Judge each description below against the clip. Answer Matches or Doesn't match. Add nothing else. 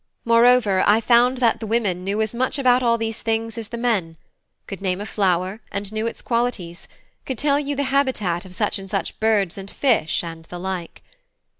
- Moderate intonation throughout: Matches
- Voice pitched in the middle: Doesn't match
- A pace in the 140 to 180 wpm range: Doesn't match